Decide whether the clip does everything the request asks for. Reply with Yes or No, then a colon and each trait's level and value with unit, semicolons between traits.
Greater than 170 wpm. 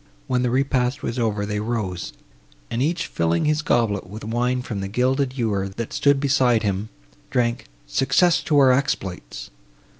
No: average, 160 wpm